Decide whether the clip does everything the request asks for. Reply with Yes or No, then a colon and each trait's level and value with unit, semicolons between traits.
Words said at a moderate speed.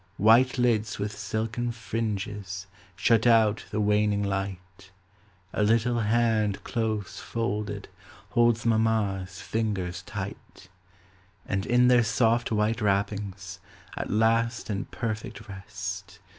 No: slow, 110 wpm